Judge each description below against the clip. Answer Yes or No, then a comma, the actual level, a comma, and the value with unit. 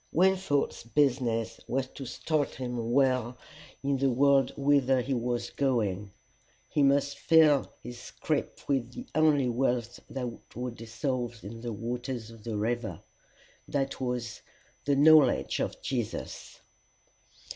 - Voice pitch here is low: Yes, low, 125 Hz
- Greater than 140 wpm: No, slow, 135 wpm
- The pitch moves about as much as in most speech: Yes, average, 3.0 semitones